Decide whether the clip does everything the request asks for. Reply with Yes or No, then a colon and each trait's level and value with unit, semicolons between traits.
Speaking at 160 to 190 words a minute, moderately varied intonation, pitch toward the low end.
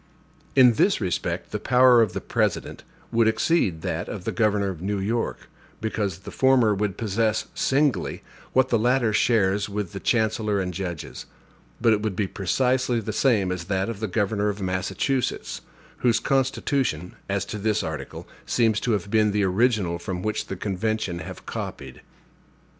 Yes: average, 170 wpm; average, 3.4 semitones; low, 105 Hz